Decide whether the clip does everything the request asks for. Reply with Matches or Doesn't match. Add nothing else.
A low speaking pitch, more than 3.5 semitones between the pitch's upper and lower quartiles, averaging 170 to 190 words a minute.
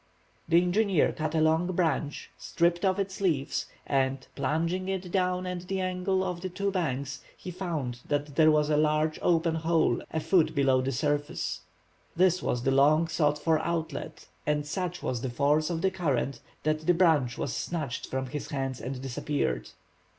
Doesn't match